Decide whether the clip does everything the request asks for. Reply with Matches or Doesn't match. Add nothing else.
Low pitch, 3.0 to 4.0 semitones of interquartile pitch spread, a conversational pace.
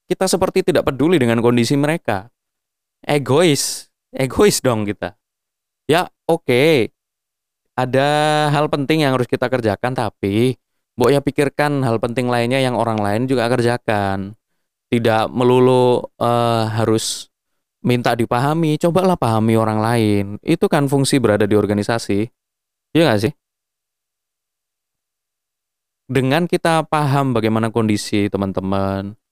Doesn't match